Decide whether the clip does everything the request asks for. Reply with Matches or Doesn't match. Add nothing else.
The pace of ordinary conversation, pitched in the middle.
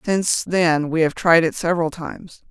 Matches